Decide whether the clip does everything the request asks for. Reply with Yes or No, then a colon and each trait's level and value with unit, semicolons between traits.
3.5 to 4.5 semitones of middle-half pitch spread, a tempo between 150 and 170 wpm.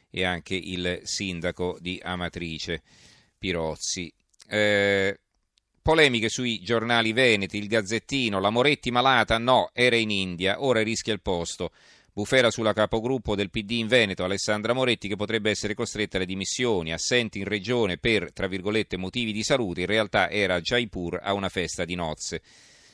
Yes: average, 3.9 semitones; average, 155 wpm